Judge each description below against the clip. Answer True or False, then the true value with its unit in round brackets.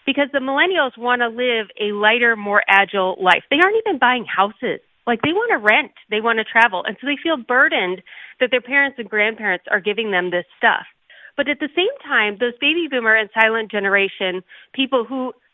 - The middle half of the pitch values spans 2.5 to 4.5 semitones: False (5.1 semitones)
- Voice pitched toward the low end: False (235 Hz)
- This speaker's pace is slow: False (205 wpm)